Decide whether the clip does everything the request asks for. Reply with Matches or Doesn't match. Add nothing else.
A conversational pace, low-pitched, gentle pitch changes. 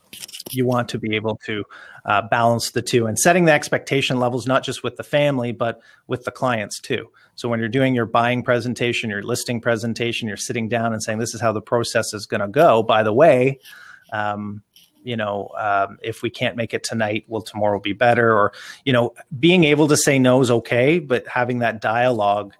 Doesn't match